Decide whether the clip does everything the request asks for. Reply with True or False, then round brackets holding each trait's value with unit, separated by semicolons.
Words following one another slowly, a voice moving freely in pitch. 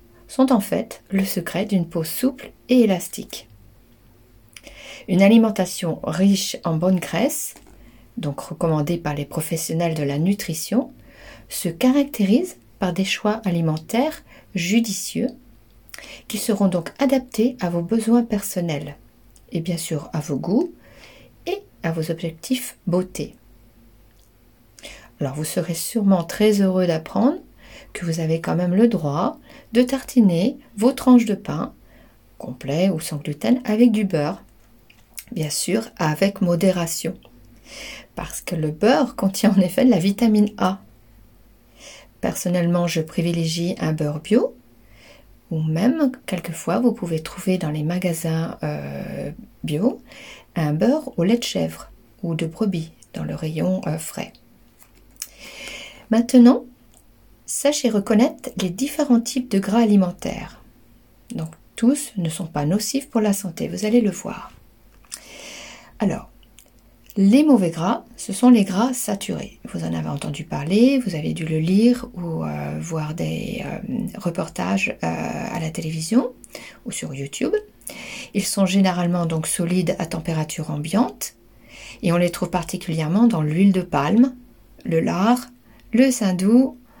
True (135 wpm; 6.7 semitones)